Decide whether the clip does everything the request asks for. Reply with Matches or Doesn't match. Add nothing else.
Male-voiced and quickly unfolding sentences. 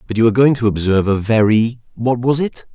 Matches